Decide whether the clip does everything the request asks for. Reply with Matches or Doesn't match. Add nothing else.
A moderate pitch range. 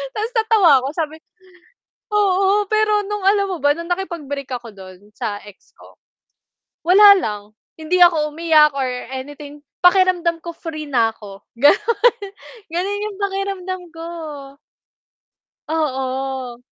Doesn't match